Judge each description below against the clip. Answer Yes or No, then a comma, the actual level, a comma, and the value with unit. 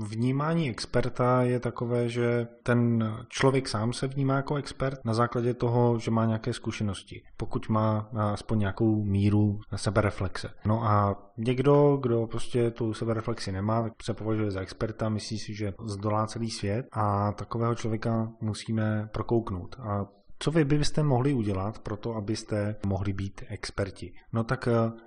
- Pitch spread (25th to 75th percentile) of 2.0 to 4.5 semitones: Yes, narrow, 2.4 semitones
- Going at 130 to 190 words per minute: Yes, average, 150 wpm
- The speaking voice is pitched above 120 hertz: No, low, 115 Hz